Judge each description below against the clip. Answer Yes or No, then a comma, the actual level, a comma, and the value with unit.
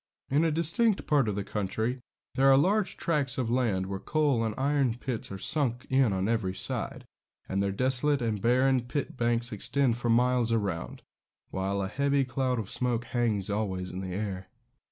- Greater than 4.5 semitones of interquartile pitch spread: Yes, average, 4.9 semitones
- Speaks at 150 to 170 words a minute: No, average, 180 wpm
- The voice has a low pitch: Yes, low, 120 Hz